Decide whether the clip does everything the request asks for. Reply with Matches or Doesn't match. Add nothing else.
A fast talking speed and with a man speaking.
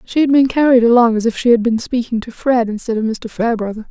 Doesn't match